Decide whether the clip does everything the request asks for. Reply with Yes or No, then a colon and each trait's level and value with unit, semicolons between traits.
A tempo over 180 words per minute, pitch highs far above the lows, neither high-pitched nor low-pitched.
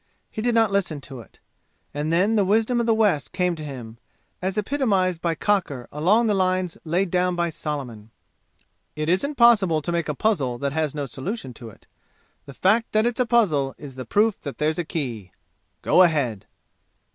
Yes: average, 190 wpm; wide, 6.6 semitones; medium, 170 Hz